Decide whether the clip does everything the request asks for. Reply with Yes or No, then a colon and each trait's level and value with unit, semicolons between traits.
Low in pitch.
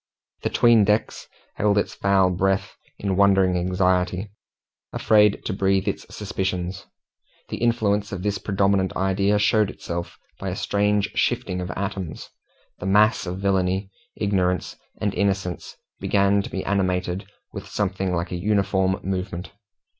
Yes: very low, 95 Hz